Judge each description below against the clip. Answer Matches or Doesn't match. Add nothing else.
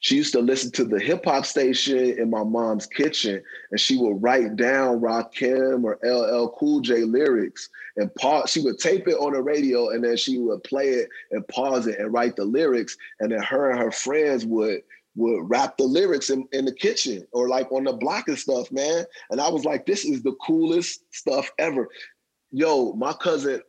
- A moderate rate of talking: Doesn't match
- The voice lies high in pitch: Doesn't match